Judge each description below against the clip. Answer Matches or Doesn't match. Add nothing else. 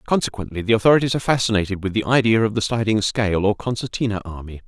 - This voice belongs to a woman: Doesn't match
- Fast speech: Doesn't match